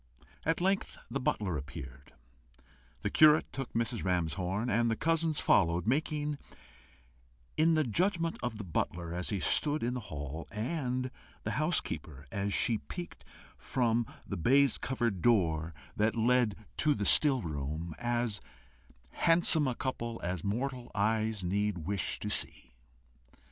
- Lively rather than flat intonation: Yes, wide, 6.8 semitones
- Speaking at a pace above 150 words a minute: No, average, 140 wpm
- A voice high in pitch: No, low, 115 Hz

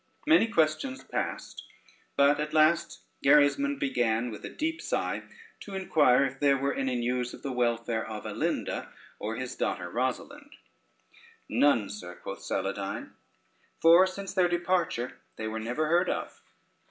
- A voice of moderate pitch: Yes, medium, 145 Hz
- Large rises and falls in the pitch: Yes, wide, 6.6 semitones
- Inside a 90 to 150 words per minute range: Yes, average, 145 wpm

